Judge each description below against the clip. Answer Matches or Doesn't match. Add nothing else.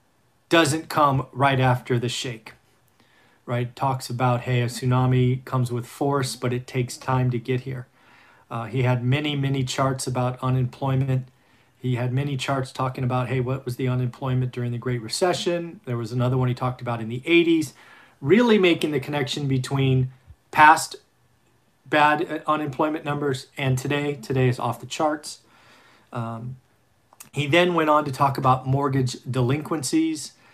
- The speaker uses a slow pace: Doesn't match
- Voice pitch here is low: Matches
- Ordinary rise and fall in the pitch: Doesn't match